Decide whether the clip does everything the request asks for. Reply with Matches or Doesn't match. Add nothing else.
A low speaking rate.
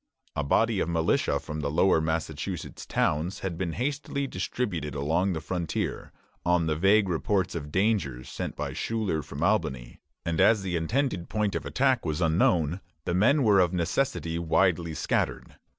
Doesn't match